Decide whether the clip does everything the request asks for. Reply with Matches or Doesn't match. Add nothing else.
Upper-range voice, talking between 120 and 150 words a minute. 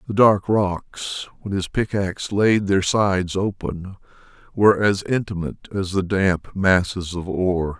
Doesn't match